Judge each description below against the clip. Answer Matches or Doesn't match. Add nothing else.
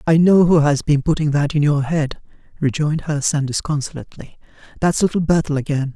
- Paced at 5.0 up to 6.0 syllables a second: Matches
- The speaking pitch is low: Doesn't match